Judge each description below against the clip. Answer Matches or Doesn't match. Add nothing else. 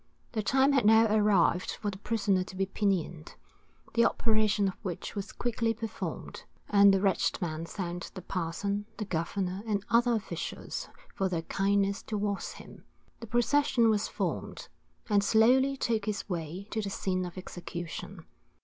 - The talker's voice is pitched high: Matches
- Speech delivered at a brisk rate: Doesn't match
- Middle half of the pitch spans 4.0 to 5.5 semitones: Doesn't match